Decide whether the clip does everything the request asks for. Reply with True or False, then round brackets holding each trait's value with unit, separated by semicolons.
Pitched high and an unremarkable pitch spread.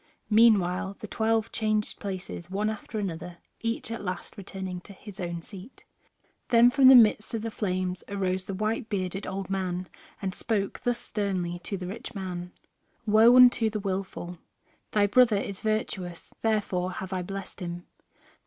True (195 Hz; 3.0 semitones)